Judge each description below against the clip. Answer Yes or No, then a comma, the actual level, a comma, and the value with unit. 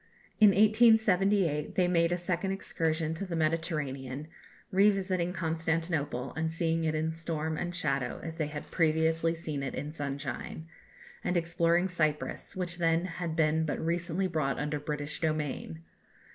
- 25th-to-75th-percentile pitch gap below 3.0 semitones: Yes, narrow, 2.5 semitones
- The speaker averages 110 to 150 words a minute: Yes, average, 145 wpm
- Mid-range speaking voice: Yes, medium, 165 Hz